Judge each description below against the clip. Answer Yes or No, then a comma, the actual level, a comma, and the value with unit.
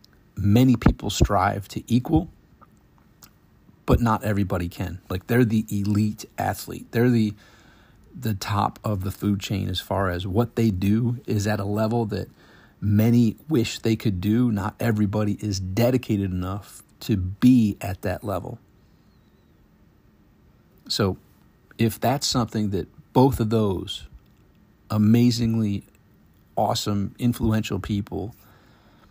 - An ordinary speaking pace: No, slow, 125 wpm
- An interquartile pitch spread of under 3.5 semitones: Yes, narrow, 2.5 semitones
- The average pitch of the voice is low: Yes, low, 105 Hz